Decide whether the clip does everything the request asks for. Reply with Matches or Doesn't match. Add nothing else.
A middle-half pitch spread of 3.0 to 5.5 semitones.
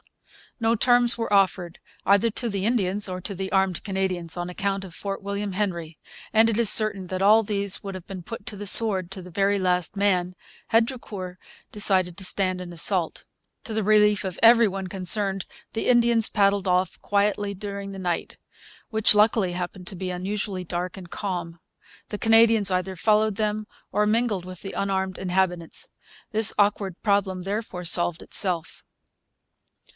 Doesn't match